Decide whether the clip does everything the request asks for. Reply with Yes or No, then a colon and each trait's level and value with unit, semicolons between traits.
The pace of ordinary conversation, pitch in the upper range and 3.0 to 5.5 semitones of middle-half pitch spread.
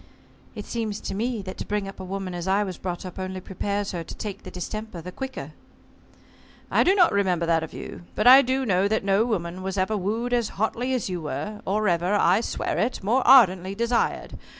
No: fast, 220 wpm; high, 200 Hz; average, 3.4 semitones